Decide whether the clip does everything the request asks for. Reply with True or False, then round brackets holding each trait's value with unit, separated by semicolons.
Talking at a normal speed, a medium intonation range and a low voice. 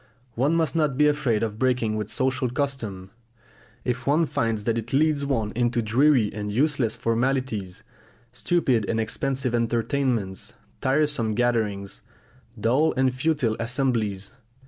False (130 wpm; 3.8 semitones; 120 Hz)